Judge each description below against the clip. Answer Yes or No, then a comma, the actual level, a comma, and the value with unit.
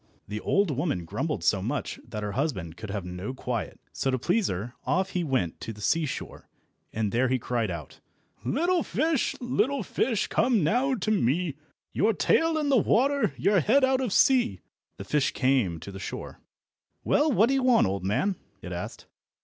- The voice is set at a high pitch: No, medium, 155 Hz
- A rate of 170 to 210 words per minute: Yes, average, 190 wpm